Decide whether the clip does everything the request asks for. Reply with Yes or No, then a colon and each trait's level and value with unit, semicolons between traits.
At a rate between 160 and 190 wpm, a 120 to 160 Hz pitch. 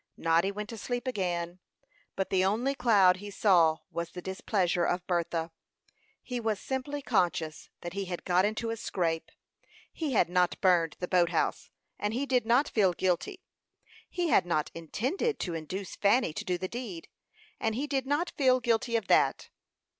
No: average, 175 wpm; high, 195 Hz